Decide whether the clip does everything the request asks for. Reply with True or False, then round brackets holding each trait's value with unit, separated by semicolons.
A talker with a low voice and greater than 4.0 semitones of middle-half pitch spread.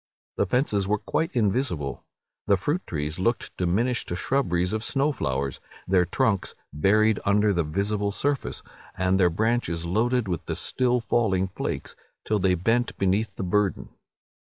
True (100 Hz; 4.6 semitones)